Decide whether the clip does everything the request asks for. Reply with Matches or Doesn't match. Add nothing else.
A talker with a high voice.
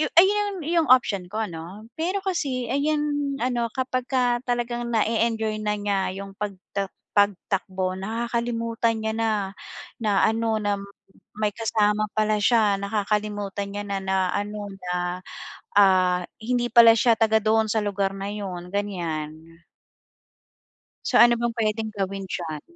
Matches